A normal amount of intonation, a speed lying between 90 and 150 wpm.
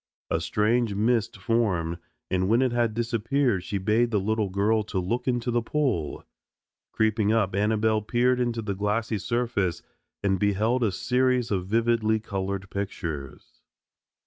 Yes: average, 3.1 semitones; average, 145 wpm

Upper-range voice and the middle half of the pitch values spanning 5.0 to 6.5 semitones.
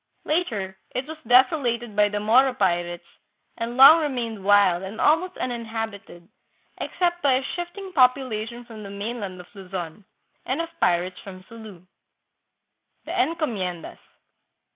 Yes: high, 225 Hz; wide, 5.4 semitones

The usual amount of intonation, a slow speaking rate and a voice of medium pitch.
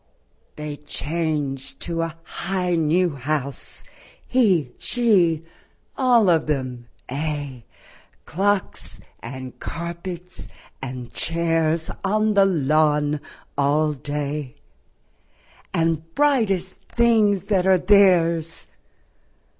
Yes: average, 4.3 semitones; slow, 85 wpm; medium, 165 Hz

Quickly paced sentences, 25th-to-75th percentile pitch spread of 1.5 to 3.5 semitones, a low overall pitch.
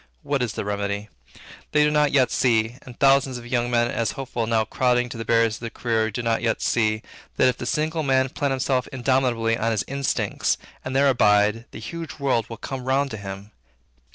Yes: fast, 210 wpm; average, 3.0 semitones; low, 120 Hz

